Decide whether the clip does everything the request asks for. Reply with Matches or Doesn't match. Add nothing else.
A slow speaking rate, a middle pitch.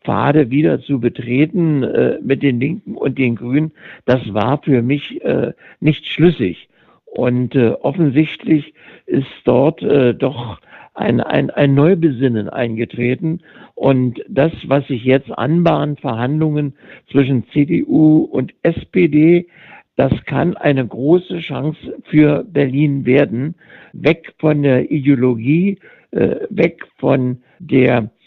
Matches